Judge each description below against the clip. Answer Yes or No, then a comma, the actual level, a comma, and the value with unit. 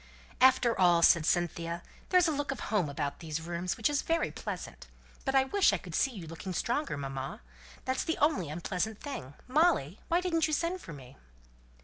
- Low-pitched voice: No, high, 205 Hz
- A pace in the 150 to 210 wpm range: Yes, average, 195 wpm